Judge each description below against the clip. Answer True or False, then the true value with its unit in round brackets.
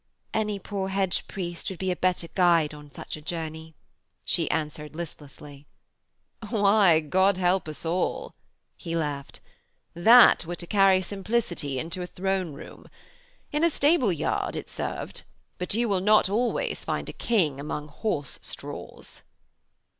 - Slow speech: False (145 wpm)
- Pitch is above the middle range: False (180 Hz)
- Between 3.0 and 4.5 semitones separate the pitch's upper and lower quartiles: True (4.0 semitones)